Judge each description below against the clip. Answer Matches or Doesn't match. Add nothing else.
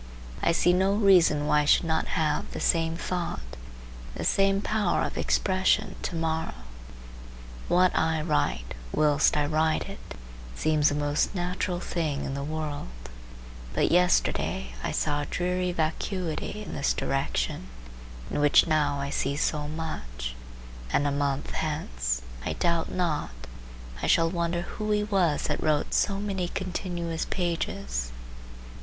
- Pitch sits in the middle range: Matches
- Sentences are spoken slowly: Doesn't match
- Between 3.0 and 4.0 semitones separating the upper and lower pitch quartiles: Matches